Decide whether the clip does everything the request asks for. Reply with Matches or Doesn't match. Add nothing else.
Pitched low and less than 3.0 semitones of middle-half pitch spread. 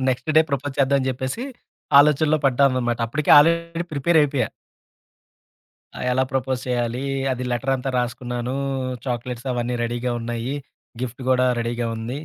Matches